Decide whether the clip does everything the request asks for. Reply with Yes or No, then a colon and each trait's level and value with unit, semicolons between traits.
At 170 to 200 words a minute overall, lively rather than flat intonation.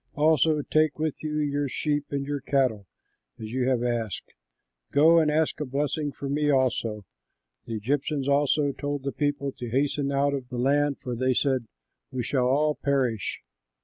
No: average, 175 wpm; narrow, 2.4 semitones